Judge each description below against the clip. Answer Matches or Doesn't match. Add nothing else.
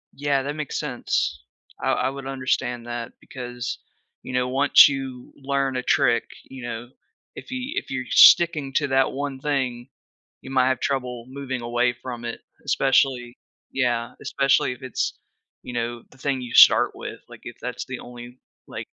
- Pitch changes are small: Matches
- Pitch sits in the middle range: Doesn't match